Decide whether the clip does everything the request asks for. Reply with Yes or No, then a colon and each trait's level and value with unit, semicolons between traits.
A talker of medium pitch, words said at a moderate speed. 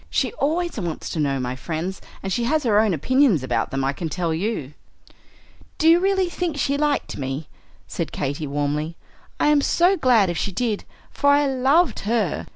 No: high, 210 Hz; average, 190 wpm